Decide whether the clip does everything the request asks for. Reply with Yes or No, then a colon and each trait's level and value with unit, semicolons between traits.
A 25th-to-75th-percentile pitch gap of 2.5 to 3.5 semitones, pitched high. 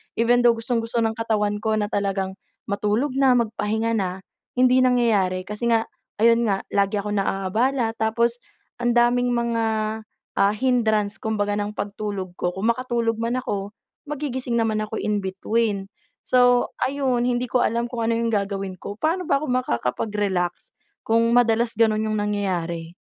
Yes: average, 2.9 semitones; high, 225 Hz